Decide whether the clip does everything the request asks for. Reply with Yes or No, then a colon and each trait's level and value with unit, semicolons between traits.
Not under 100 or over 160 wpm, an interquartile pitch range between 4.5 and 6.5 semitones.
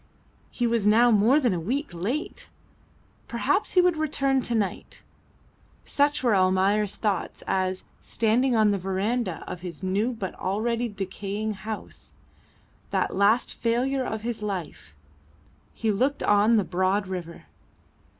No: average, 140 wpm; average, 4.1 semitones